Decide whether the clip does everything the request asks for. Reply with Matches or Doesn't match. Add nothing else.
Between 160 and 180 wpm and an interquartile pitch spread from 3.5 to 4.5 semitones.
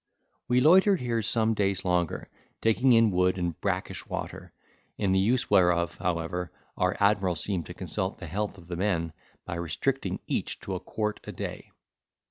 Matches